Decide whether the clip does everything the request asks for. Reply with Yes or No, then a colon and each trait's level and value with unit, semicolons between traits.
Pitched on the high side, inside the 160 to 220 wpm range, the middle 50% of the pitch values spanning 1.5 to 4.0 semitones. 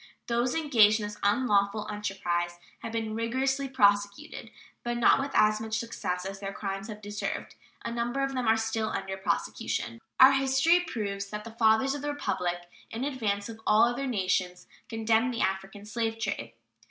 Yes: high, 220 Hz; average, 175 wpm; average, 3.2 semitones